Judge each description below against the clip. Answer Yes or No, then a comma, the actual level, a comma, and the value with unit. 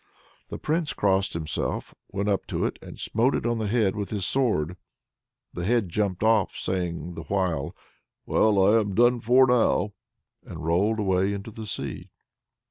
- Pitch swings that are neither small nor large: Yes, average, 3.5 semitones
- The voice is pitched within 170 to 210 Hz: No, low, 100 Hz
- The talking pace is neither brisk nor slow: Yes, average, 170 wpm